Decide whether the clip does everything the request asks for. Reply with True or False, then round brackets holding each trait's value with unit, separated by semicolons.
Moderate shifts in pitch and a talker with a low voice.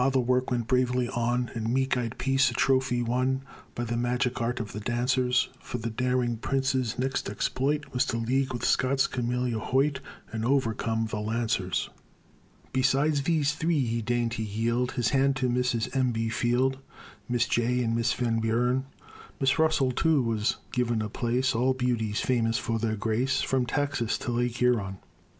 False (2.1 semitones; 125 Hz)